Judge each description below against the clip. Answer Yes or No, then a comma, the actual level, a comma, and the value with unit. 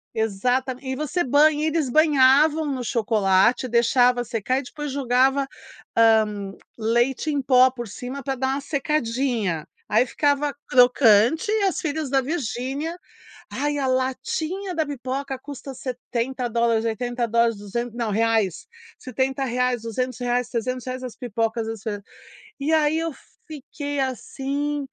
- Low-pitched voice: No, very high, 255 Hz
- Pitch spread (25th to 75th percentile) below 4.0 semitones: Yes, average, 3.3 semitones